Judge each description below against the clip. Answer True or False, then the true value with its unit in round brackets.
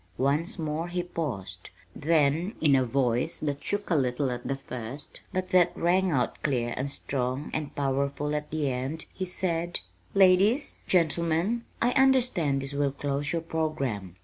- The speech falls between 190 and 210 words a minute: False (160 wpm)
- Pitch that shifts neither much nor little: True (4.2 semitones)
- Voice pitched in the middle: True (150 Hz)